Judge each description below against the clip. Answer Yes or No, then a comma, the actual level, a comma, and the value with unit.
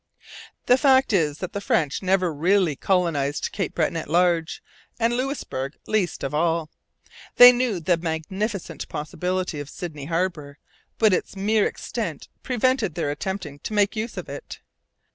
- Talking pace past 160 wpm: No, average, 150 wpm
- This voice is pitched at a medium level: Yes, medium, 180 Hz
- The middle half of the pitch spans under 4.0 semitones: No, average, 5.1 semitones